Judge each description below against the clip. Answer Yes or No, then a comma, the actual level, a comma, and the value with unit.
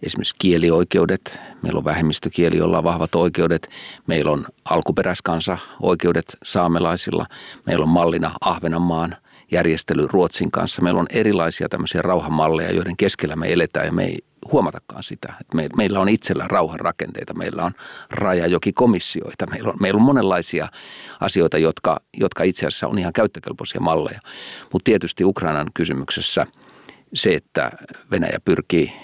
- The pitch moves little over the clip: Yes, narrow, 1.6 semitones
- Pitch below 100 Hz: Yes, very low, 85 Hz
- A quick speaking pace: No, average, 125 wpm